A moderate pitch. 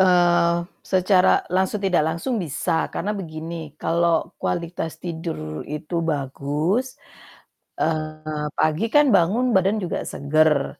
Yes: medium, 170 Hz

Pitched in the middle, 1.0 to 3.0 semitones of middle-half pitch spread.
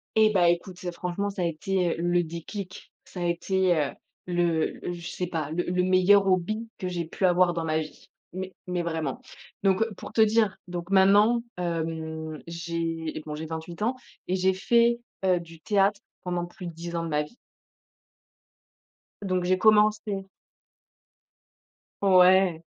Yes: medium, 180 Hz; narrow, 2.4 semitones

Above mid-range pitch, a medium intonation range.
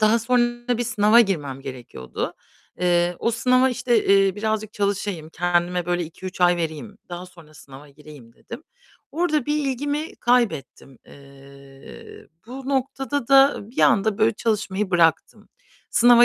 No: high, 200 Hz; wide, 6.5 semitones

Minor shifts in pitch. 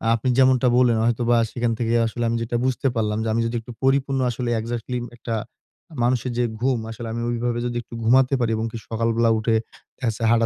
Yes: narrow, 1.5 semitones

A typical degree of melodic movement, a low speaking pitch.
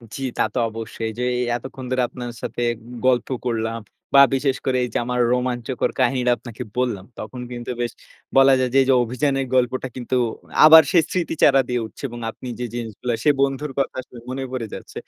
No: narrow, 1.9 semitones; low, 125 Hz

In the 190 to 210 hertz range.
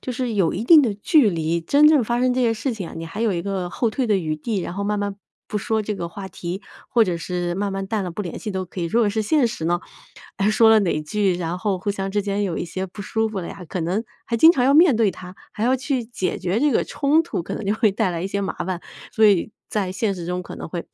Yes: high, 200 Hz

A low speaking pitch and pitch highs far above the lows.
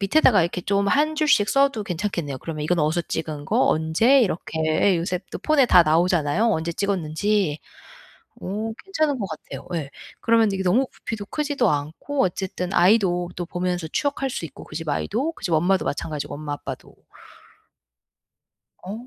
No: medium, 185 Hz; wide, 5.8 semitones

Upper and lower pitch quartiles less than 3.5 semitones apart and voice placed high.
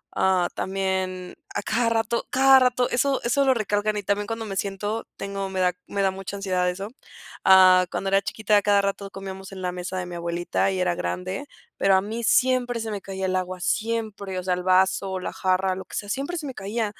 Yes: average, 3.0 semitones; high, 195 Hz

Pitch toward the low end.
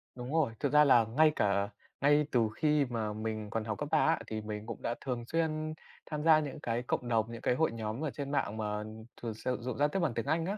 Yes: low, 125 Hz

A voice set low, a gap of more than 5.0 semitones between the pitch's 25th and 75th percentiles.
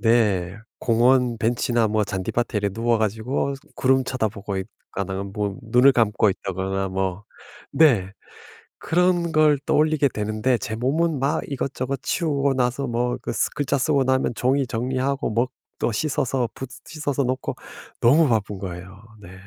No: low, 120 Hz; average, 4.7 semitones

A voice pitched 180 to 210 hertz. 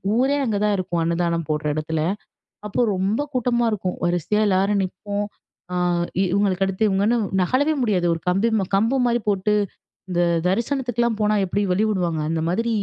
Yes: high, 200 Hz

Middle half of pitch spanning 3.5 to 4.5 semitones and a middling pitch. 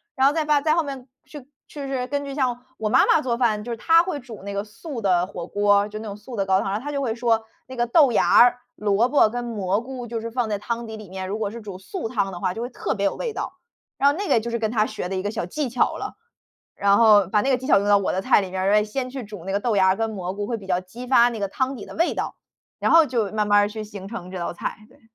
No: average, 4.1 semitones; high, 225 Hz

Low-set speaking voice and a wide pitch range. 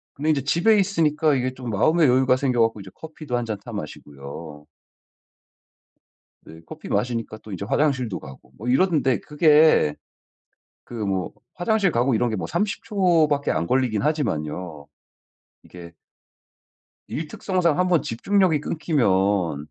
Yes: low, 130 Hz; wide, 7.8 semitones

